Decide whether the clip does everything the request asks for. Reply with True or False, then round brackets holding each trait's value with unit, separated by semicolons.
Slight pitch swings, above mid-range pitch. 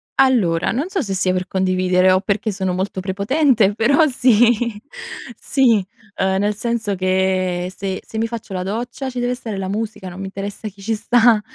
False (3.8 semitones; 205 Hz)